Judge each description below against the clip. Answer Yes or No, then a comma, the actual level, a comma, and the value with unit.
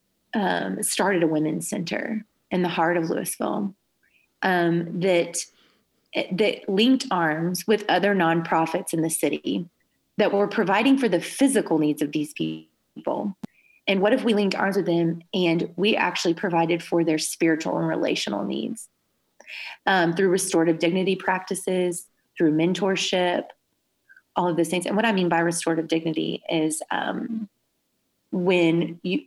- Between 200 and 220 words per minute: No, average, 145 wpm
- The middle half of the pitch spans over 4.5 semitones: No, average, 3.2 semitones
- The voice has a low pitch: No, medium, 180 Hz